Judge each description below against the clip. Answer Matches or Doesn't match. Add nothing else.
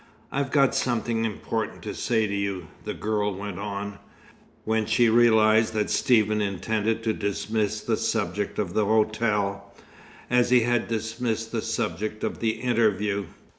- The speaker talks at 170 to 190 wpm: Doesn't match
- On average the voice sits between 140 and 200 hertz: Doesn't match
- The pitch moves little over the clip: Matches